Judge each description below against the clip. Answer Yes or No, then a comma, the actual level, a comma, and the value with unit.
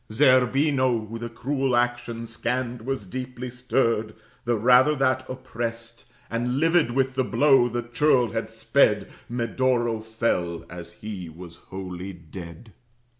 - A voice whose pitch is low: Yes, low, 120 Hz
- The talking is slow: Yes, slow, 130 wpm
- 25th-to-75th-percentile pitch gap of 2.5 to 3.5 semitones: Yes, average, 2.9 semitones